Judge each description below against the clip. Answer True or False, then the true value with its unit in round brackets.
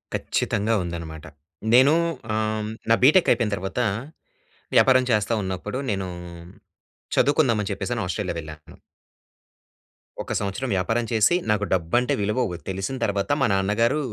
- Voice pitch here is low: True (105 Hz)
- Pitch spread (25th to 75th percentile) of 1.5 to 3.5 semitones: False (4.0 semitones)